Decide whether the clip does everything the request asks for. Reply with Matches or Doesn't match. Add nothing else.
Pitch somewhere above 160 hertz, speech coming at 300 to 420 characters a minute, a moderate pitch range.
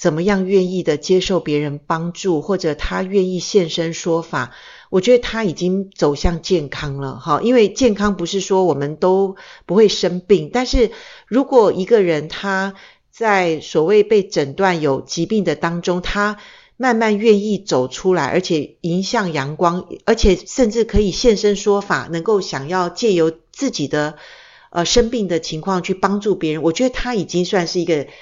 Doesn't match